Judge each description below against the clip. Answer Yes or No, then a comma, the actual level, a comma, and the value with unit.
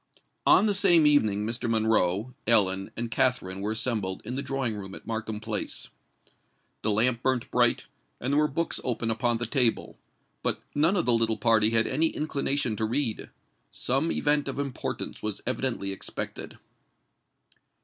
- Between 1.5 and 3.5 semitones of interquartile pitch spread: No, average, 3.9 semitones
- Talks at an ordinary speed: Yes, average, 160 wpm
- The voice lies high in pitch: No, low, 120 Hz